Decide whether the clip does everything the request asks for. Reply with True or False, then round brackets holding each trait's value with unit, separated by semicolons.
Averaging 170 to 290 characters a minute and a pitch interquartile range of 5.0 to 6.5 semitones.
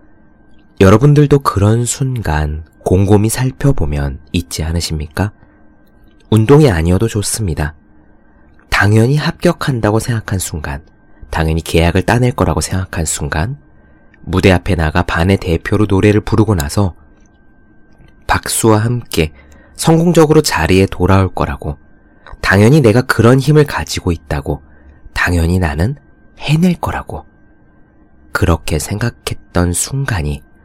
True (265 characters per minute; 5.5 semitones)